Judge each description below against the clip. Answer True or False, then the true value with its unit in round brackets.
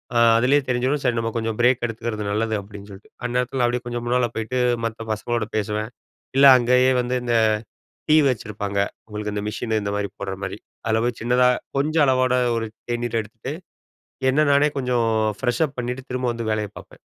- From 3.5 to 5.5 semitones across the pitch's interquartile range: False (2.6 semitones)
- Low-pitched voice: True (120 Hz)